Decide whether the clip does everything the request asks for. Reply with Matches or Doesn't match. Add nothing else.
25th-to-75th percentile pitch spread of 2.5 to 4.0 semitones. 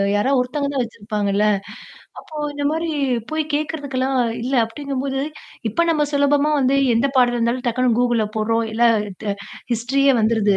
Matches